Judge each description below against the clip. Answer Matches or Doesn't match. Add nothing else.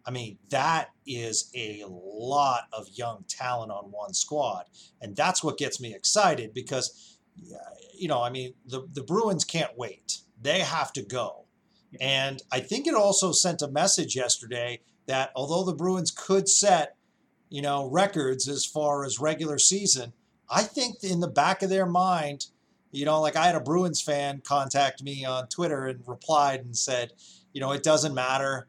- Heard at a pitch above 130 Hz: Matches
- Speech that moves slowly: Doesn't match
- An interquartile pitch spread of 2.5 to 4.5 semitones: Doesn't match